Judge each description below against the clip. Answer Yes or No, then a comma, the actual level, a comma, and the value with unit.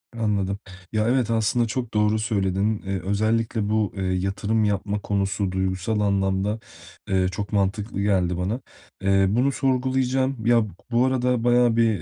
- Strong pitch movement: No, average, 3.1 semitones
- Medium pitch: No, low, 105 Hz